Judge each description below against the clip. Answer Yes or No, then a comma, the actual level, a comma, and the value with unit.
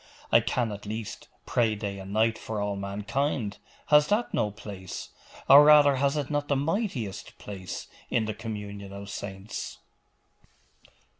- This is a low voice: Yes, low, 110 Hz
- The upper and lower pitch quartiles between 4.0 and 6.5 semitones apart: Yes, wide, 5.6 semitones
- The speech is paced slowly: No, average, 150 wpm